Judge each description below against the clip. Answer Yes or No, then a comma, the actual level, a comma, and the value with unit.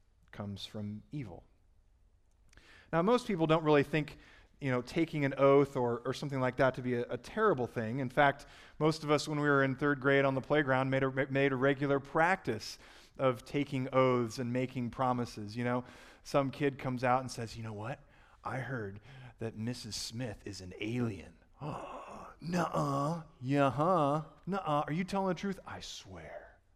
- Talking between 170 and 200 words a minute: Yes, average, 180 wpm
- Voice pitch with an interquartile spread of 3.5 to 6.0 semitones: Yes, average, 3.9 semitones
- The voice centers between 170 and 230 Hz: No, low, 130 Hz